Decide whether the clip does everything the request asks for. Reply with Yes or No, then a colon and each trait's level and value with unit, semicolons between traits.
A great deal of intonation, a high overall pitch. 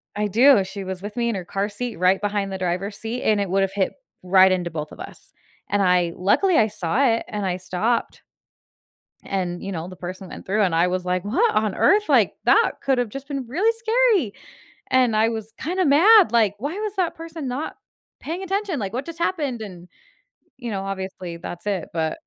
Yes: wide, 6.9 semitones; high, 210 Hz